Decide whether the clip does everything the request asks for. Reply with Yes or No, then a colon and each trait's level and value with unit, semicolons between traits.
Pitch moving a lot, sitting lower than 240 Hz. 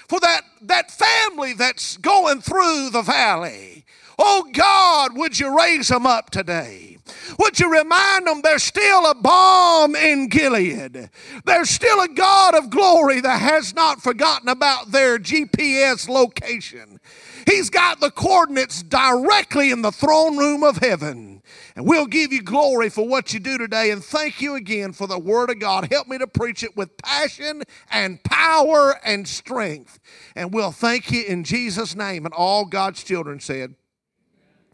No: wide, 6.3 semitones; very high, 275 Hz